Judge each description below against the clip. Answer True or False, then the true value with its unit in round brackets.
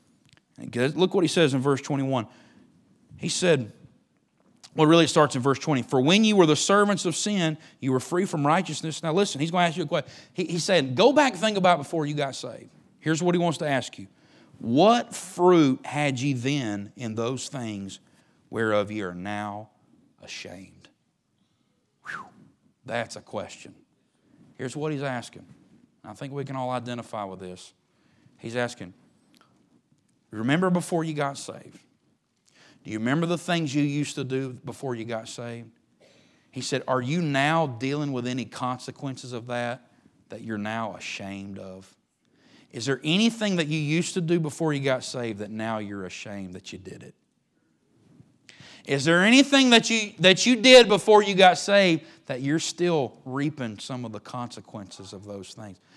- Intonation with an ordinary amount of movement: False (6.1 semitones)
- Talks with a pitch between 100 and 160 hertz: True (140 Hz)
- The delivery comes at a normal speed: True (175 wpm)